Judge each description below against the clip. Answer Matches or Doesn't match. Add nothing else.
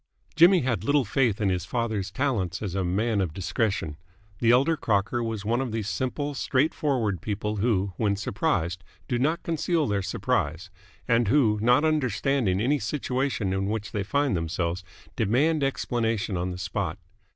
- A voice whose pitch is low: Matches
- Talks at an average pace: Matches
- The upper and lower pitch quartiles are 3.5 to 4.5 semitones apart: Doesn't match